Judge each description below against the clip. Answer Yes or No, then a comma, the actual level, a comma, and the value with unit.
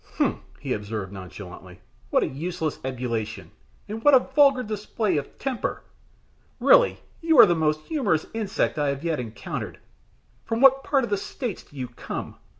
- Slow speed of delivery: No, average, 165 wpm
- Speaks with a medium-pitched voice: Yes, medium, 170 Hz